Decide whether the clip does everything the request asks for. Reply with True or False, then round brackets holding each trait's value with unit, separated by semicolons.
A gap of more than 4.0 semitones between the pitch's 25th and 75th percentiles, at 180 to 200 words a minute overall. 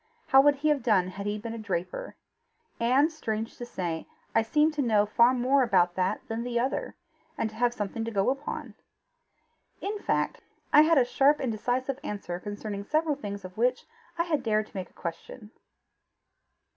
True (4.9 semitones; 190 wpm)